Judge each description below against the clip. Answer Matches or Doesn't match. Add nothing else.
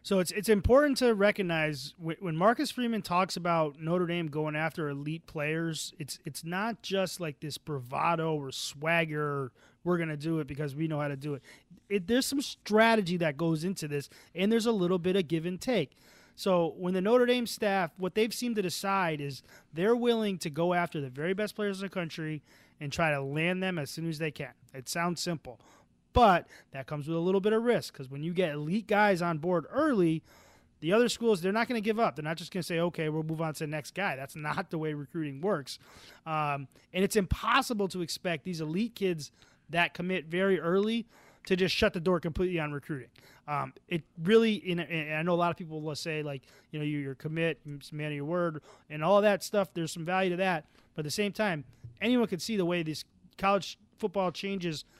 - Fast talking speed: Matches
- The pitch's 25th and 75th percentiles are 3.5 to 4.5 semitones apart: Matches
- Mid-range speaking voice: Matches